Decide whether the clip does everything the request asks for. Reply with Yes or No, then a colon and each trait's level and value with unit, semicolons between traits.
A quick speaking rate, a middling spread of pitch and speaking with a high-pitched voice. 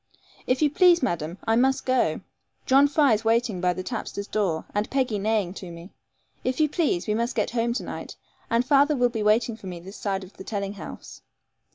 Yes: fast, 215 wpm; average, 4.9 semitones; high, 225 Hz